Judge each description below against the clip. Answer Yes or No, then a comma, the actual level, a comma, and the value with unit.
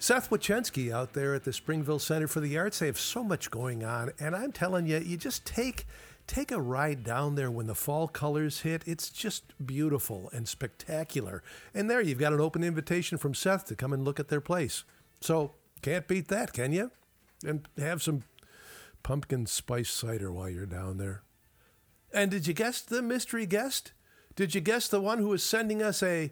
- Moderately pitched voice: Yes, medium, 155 Hz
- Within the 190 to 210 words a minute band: Yes, average, 200 wpm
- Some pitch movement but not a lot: No, wide, 6.5 semitones